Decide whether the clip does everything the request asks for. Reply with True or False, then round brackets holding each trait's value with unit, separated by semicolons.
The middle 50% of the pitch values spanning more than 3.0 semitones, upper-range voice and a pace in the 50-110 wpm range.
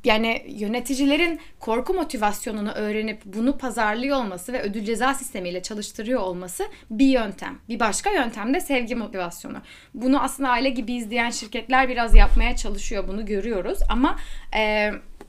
False (3.6 semitones; 235 Hz; 135 wpm)